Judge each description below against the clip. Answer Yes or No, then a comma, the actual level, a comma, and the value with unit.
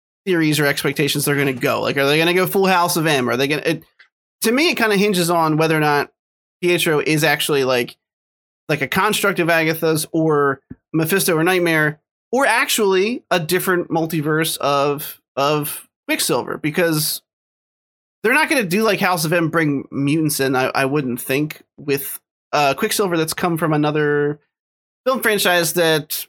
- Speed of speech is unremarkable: Yes, average, 180 wpm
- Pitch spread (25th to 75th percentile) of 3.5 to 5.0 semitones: Yes, average, 3.8 semitones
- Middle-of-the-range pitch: Yes, medium, 160 Hz